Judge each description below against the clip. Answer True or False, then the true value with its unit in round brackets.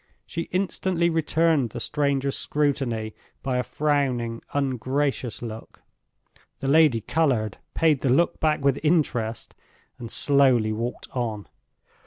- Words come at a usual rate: False (120 wpm)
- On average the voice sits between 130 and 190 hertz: True (135 Hz)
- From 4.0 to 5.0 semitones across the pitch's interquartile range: True (4.3 semitones)